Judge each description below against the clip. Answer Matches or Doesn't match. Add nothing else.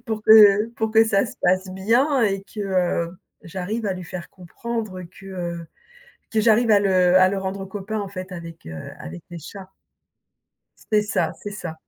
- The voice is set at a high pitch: Matches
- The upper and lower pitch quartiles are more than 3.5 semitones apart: Doesn't match